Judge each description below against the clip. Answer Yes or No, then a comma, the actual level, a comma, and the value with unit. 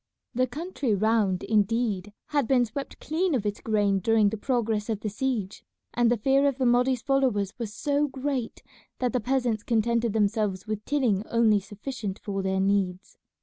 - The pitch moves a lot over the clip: No, average, 3.8 semitones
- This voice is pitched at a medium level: No, high, 225 Hz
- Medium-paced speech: Yes, average, 175 wpm